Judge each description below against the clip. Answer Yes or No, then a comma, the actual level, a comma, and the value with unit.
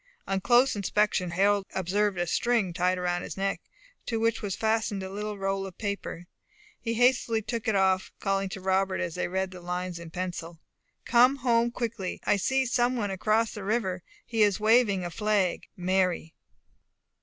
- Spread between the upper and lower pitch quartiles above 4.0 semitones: No, average, 3.4 semitones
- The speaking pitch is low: No, high, 195 Hz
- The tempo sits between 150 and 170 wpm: No, average, 180 wpm